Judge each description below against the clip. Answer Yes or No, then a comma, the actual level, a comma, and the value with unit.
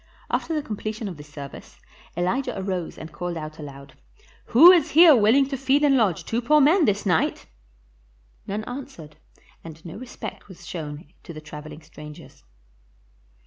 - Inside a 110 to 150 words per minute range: No, average, 160 wpm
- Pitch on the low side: No, high, 195 Hz